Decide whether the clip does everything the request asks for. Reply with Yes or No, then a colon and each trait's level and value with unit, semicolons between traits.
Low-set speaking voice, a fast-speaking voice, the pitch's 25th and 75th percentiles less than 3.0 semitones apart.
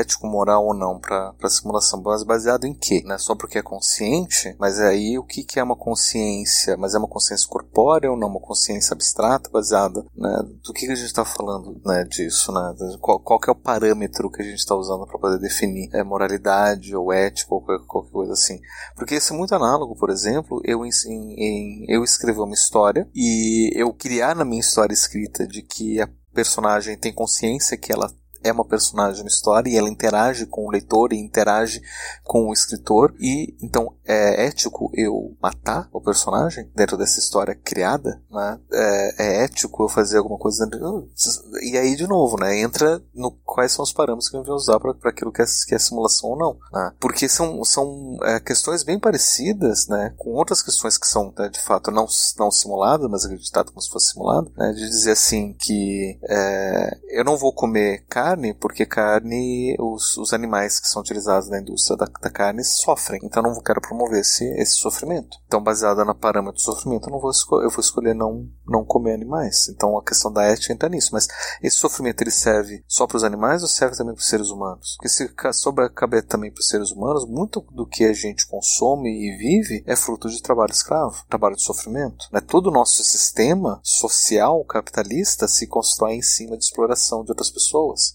Yes: low, 110 Hz; fast, 205 wpm; narrow, 2.6 semitones